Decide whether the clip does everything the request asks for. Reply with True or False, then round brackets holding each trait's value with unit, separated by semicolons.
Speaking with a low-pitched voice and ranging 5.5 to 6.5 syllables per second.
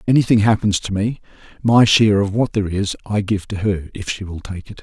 True (105 Hz; 6.1 syllables/s)